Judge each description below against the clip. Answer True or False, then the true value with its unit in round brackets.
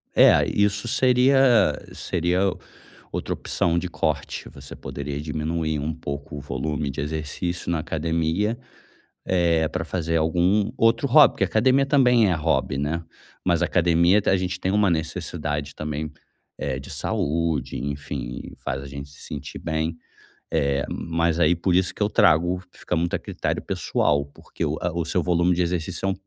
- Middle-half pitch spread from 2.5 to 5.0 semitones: True (3.5 semitones)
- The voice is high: False (85 Hz)